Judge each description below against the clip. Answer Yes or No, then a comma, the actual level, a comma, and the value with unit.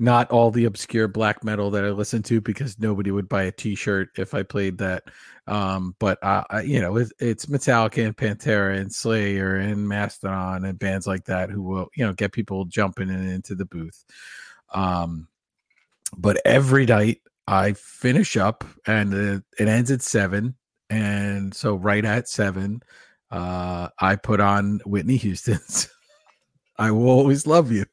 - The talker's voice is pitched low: Yes, low, 105 Hz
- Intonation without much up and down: No, average, 3.0 semitones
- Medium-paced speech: Yes, average, 170 wpm